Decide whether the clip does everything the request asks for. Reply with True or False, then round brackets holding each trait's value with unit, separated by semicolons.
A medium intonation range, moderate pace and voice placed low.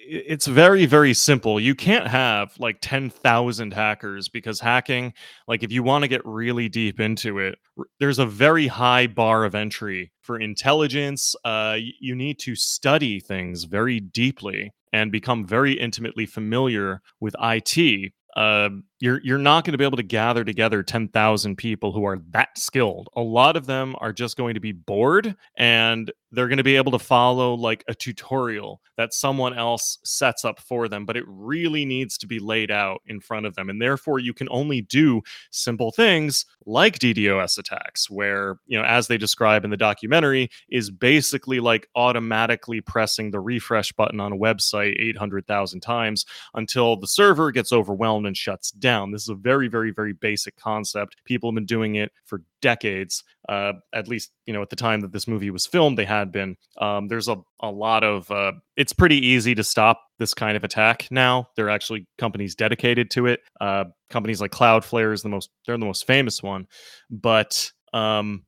True (3.1 semitones; 185 wpm; 115 Hz)